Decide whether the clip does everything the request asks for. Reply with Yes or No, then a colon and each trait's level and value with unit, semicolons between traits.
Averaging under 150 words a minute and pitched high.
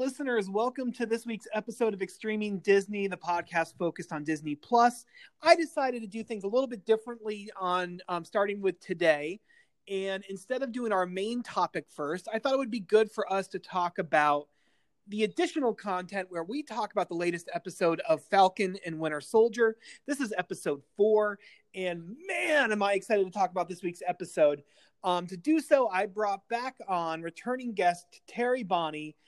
No: average, 185 wpm; high, 200 Hz